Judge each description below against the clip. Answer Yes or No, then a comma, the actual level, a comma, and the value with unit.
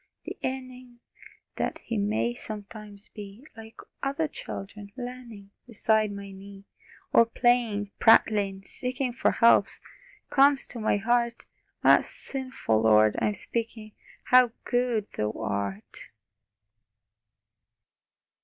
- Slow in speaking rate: Yes, slow, 105 wpm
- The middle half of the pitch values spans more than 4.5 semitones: No, average, 3.5 semitones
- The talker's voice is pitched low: No, high, 220 Hz